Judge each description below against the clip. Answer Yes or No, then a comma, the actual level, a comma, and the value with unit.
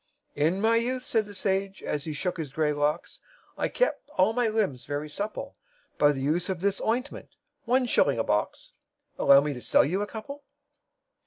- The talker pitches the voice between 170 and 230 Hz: Yes, high, 190 Hz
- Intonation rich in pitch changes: Yes, wide, 7.2 semitones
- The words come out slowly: No, average, 190 wpm